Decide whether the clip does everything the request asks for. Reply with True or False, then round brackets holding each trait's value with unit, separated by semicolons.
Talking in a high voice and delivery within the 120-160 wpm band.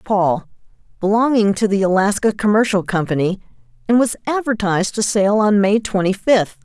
True (205 Hz; 145 wpm)